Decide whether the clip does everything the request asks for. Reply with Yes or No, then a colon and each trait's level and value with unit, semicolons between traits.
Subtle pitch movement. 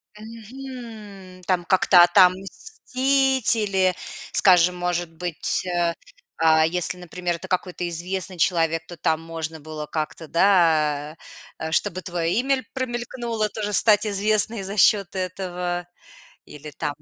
No: average, 3.8 semitones